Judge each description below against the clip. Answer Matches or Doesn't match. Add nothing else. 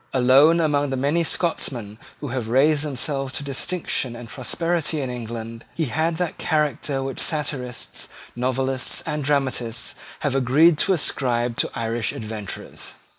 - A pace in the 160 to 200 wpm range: Doesn't match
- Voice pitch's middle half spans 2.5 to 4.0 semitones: Matches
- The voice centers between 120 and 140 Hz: Matches